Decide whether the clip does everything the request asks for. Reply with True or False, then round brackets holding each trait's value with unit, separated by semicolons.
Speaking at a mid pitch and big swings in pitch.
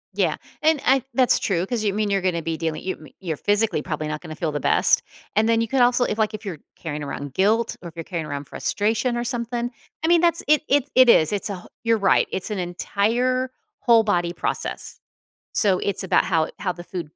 False (205 Hz; 5.8 semitones)